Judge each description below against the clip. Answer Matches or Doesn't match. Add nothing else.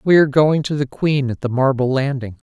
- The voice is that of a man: Matches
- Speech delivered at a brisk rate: Matches